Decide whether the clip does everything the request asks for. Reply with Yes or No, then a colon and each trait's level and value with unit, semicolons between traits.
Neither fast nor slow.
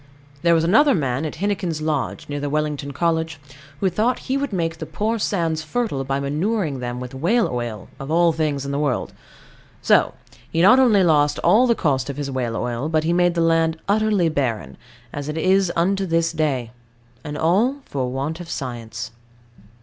Yes: average, 190 wpm